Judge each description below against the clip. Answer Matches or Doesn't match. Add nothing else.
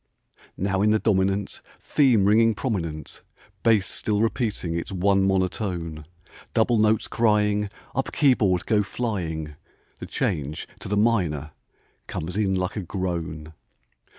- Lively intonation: Doesn't match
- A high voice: Doesn't match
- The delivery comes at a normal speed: Doesn't match